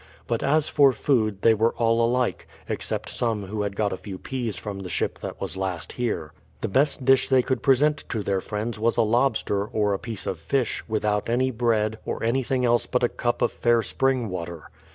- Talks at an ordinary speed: No, fast, 215 wpm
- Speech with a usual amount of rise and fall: Yes, average, 3.4 semitones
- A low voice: Yes, low, 115 Hz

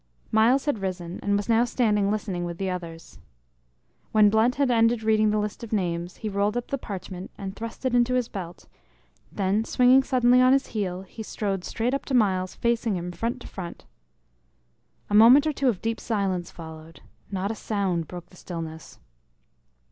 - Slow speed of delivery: No, average, 185 wpm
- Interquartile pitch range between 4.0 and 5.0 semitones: Yes, average, 4.3 semitones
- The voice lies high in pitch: Yes, high, 210 Hz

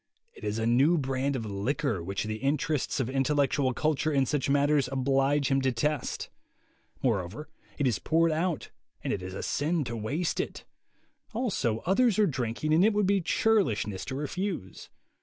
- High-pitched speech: No, medium, 140 Hz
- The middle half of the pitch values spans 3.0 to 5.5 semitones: Yes, average, 5.0 semitones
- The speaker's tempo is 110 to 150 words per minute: No, average, 170 wpm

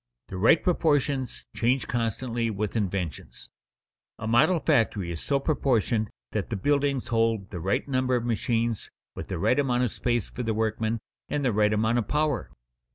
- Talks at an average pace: Yes, average, 170 wpm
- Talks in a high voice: No, low, 115 Hz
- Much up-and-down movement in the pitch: No, average, 3.6 semitones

